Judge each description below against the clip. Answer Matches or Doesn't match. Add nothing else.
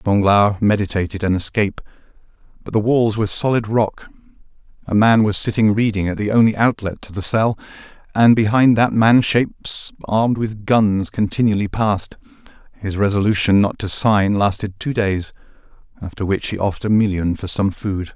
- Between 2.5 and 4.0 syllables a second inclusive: Doesn't match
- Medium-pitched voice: Doesn't match